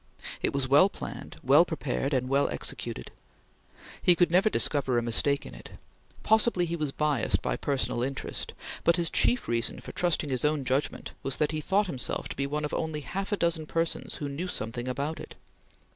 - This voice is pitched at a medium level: Yes, medium, 150 Hz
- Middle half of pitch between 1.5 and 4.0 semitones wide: No, average, 4.4 semitones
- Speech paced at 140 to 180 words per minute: No, average, 195 wpm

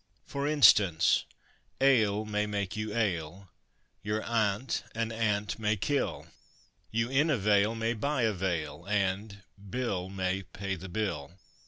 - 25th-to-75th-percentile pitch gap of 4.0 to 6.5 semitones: No, average, 2.9 semitones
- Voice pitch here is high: No, low, 105 Hz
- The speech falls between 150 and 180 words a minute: No, average, 140 wpm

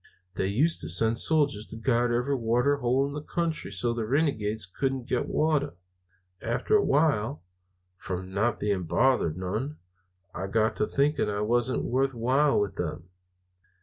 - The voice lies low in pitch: Yes, low, 120 Hz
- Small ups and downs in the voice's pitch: No, average, 5.1 semitones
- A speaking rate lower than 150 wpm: No, average, 160 wpm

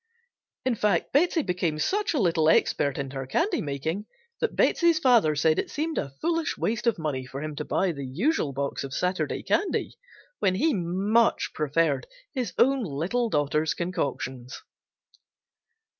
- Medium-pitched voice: Yes, medium, 175 Hz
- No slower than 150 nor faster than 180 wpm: Yes, average, 160 wpm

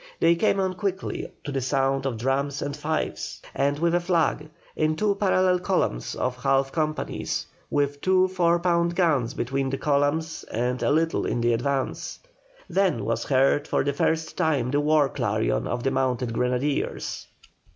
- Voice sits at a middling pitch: Yes, medium, 145 Hz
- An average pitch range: Yes, average, 4.2 semitones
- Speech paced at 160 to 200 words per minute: Yes, average, 165 wpm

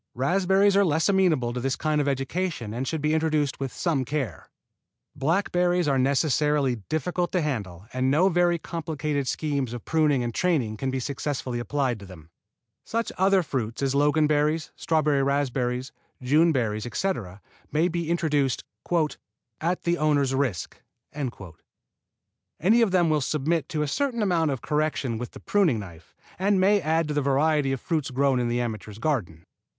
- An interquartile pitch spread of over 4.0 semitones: Yes, average, 4.4 semitones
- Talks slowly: No, average, 165 wpm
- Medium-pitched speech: Yes, medium, 145 Hz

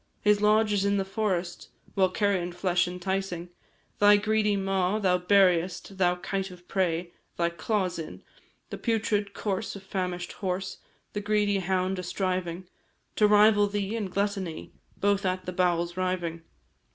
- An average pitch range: No, narrow, 2.3 semitones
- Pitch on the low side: No, high, 190 Hz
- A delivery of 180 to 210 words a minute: No, average, 150 wpm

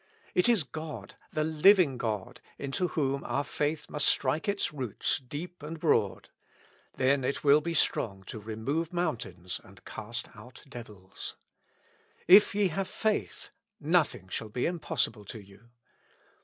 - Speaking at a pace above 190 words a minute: No, average, 145 wpm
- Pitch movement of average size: No, wide, 6.5 semitones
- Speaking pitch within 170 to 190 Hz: No, medium, 140 Hz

